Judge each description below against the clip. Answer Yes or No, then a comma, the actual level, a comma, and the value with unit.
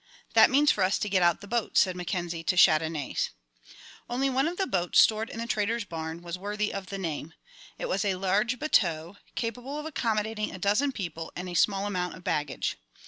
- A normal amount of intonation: Yes, average, 4.7 semitones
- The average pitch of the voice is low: No, high, 200 Hz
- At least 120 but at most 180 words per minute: No, fast, 205 wpm